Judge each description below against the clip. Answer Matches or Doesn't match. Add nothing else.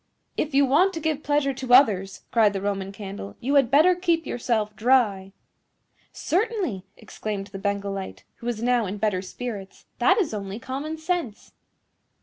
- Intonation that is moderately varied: Doesn't match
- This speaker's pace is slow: Doesn't match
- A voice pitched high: Matches